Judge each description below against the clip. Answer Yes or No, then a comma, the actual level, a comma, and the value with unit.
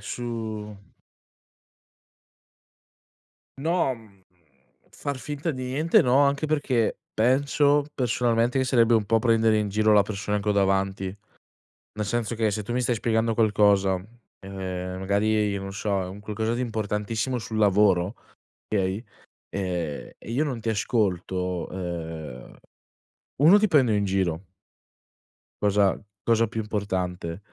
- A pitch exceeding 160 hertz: No, low, 105 Hz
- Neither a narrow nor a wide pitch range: Yes, average, 3.5 semitones